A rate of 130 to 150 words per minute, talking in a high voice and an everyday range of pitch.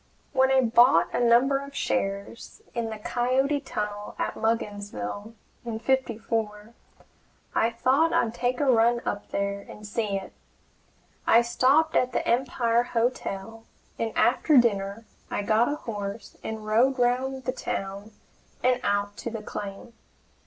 Yes: average, 145 wpm; high, 230 Hz; average, 3.3 semitones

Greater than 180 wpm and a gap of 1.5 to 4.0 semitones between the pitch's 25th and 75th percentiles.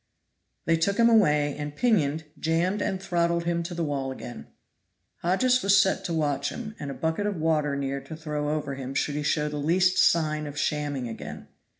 Yes: average, 200 wpm; average, 3.2 semitones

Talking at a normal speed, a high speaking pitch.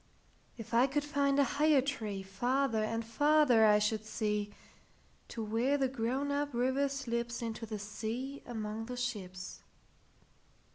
No: slow, 130 wpm; high, 235 Hz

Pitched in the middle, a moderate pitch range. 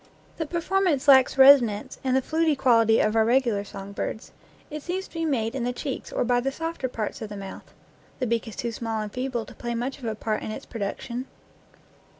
No: high, 245 Hz; average, 3.6 semitones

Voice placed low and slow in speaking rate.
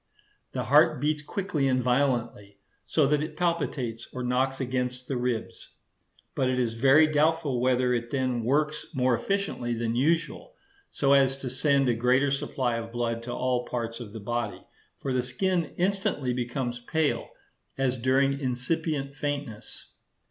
No: low, 130 Hz; average, 155 wpm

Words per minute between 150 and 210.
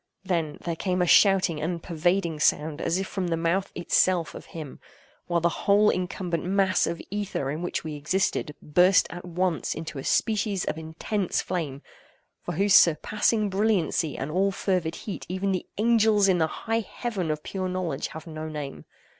Yes: average, 180 wpm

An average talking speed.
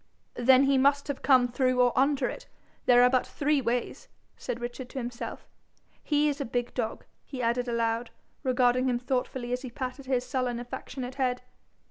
Yes: average, 175 wpm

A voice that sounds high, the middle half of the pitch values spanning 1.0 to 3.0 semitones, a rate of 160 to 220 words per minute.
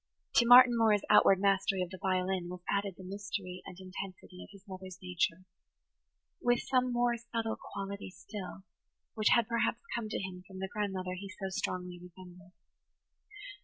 Yes: high, 195 Hz; average, 2.7 semitones; average, 165 wpm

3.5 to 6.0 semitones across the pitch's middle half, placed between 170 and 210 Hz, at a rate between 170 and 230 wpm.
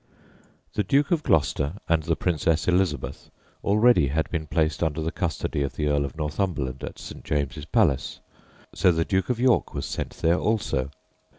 No: average, 4.5 semitones; very low, 80 Hz; average, 175 wpm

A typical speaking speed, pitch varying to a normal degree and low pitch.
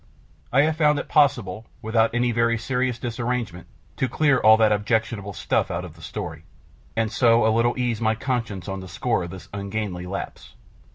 Yes: average, 185 wpm; average, 3.7 semitones; low, 115 Hz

